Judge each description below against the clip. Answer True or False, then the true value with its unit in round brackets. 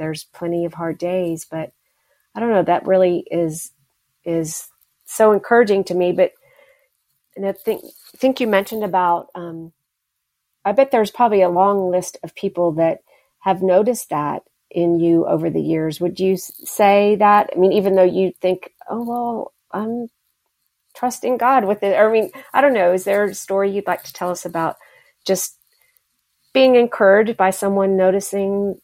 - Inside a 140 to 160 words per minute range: False (175 wpm)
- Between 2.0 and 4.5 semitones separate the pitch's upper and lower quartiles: True (3.7 semitones)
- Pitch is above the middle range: True (195 Hz)